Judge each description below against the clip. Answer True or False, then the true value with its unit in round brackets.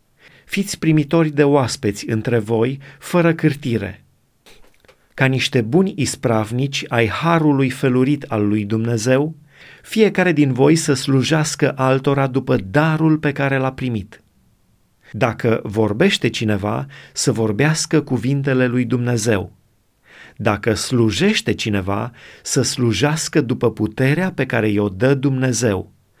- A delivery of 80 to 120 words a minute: True (115 wpm)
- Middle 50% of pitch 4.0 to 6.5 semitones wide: True (4.6 semitones)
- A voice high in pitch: False (130 Hz)